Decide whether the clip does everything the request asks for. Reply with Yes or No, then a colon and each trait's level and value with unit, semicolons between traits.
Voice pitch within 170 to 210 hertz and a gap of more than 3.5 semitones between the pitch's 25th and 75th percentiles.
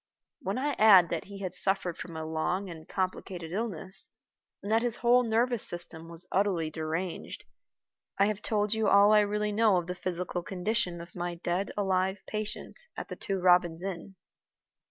No: high, 190 Hz; average, 3.2 semitones